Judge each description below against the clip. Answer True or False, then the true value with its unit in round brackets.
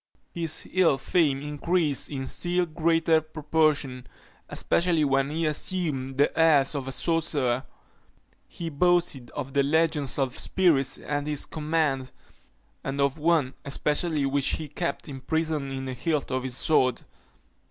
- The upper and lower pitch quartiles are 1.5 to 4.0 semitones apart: True (3.2 semitones)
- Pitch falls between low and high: True (150 Hz)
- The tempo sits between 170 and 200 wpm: False (140 wpm)